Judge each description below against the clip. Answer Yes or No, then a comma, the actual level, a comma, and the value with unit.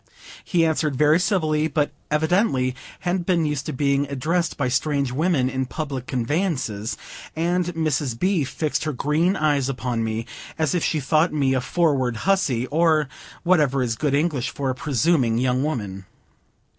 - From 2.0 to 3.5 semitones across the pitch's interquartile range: No, average, 4.0 semitones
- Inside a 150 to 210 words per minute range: Yes, average, 160 wpm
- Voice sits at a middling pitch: Yes, medium, 145 Hz